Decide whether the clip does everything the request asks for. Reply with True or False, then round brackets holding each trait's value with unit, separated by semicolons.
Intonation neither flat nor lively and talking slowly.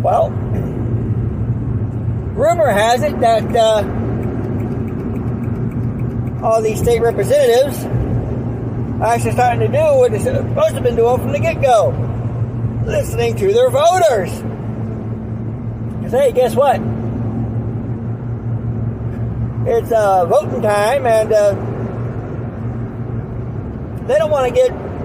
False (1.4 semitones; 110 wpm)